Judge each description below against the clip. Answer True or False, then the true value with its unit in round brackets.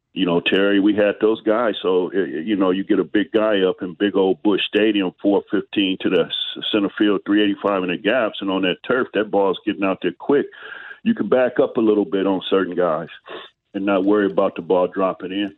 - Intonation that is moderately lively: False (1.6 semitones)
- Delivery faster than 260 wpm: False (225 wpm)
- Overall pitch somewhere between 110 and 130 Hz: False (100 Hz)